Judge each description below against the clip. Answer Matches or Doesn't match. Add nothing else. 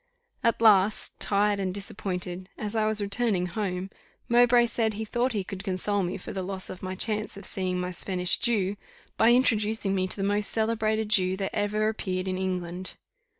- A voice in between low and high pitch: Doesn't match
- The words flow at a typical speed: Matches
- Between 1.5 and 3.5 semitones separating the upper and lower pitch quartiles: Matches